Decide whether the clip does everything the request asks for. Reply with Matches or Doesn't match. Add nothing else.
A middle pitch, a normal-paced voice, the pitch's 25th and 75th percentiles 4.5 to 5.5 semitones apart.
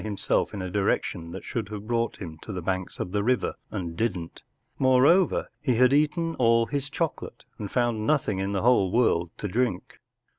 Doesn't match